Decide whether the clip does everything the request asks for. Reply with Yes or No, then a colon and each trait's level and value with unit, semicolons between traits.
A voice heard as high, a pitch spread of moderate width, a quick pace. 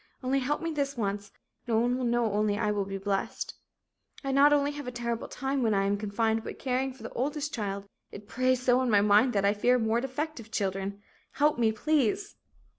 Yes: high, 235 Hz; average, 4.5 semitones; fast, 215 wpm